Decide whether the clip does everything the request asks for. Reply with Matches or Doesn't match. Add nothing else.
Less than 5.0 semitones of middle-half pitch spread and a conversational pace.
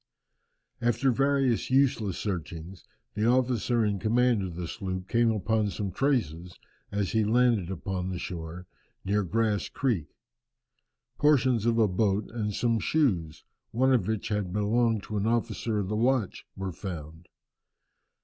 Matches